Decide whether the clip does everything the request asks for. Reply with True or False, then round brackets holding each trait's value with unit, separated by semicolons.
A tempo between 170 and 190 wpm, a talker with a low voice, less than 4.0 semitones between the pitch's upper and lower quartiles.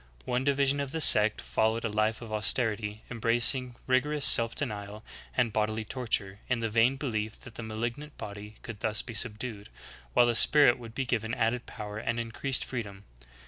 True (185 wpm; 115 Hz; 2.8 semitones)